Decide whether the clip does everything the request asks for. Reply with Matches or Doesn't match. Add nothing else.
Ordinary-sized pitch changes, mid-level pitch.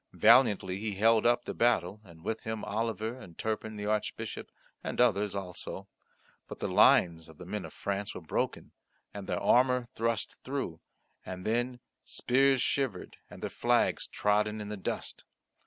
Doesn't match